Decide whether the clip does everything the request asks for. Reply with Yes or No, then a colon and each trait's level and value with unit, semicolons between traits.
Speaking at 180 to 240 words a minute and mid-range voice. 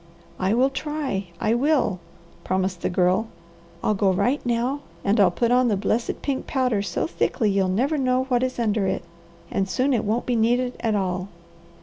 No: average, 190 wpm; high, 230 Hz